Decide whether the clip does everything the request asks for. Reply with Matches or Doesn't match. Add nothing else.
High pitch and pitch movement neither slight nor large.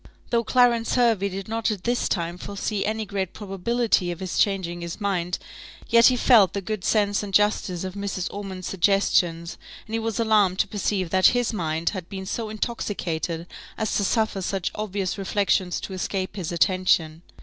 Matches